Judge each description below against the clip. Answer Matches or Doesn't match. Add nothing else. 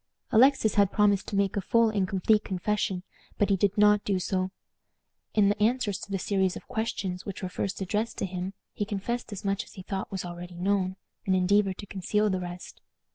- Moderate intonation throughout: Doesn't match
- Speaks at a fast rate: Matches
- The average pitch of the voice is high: Matches